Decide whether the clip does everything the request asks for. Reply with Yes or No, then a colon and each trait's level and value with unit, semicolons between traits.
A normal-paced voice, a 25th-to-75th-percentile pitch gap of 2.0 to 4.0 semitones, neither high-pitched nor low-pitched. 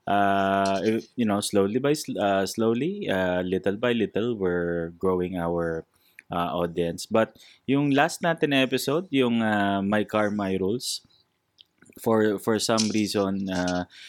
No: average, 140 wpm; average, 3.6 semitones; low, 100 Hz